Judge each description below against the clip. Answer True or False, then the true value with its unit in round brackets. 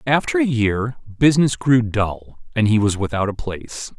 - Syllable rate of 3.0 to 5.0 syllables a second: True (4.8 syllables/s)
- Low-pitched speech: True (120 Hz)